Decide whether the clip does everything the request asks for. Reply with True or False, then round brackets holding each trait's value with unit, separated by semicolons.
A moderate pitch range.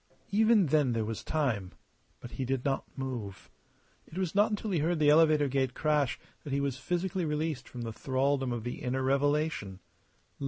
True (3.9 semitones)